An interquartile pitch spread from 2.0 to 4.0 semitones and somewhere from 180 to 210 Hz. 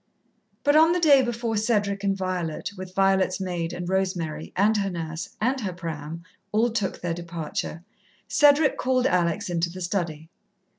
No: average, 4.4 semitones; high, 190 Hz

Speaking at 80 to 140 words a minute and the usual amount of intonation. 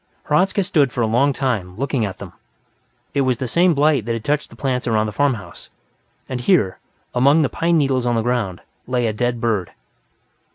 No: average, 200 wpm; average, 3.9 semitones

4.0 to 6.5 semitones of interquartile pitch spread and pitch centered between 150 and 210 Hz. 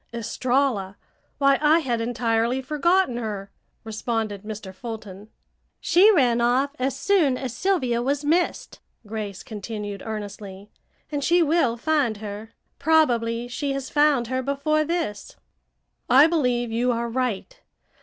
No: average, 4.6 semitones; high, 245 Hz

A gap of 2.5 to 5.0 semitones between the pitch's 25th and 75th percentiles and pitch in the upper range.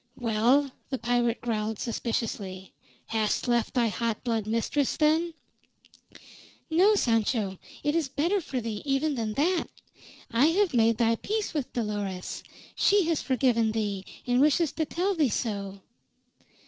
No: wide, 5.4 semitones; high, 240 Hz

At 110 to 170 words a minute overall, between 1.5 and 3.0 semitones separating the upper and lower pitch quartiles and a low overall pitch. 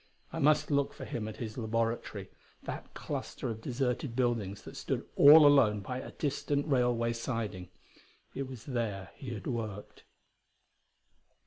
No: average, 145 wpm; average, 3.6 semitones; low, 120 Hz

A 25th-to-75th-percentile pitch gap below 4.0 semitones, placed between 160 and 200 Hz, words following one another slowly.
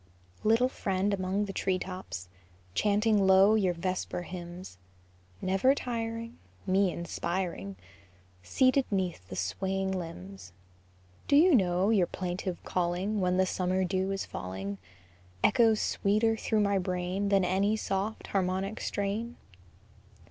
Yes: narrow, 2.6 semitones; high, 190 Hz; slow, 125 wpm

